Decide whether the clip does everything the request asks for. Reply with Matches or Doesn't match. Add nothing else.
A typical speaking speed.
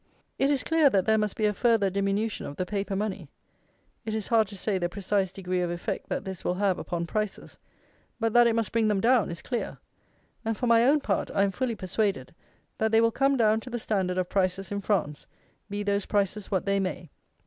Doesn't match